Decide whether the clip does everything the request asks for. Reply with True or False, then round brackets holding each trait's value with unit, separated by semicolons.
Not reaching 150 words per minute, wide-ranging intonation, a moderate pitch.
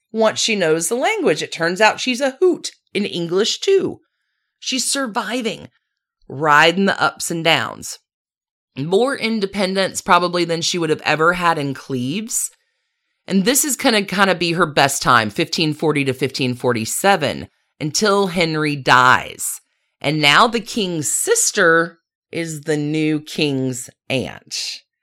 True (140 wpm; 7.8 semitones; 175 Hz)